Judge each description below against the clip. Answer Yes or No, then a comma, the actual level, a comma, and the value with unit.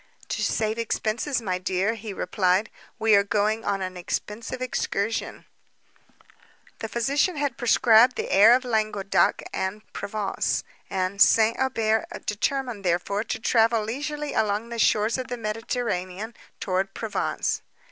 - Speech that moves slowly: Yes, slow, 130 wpm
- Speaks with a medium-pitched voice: No, high, 220 Hz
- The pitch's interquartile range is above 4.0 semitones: No, average, 2.9 semitones